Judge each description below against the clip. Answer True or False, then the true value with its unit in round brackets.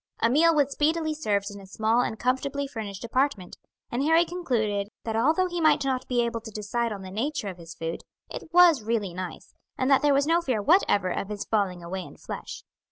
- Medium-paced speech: False (220 wpm)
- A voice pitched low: False (235 Hz)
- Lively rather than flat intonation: True (6.3 semitones)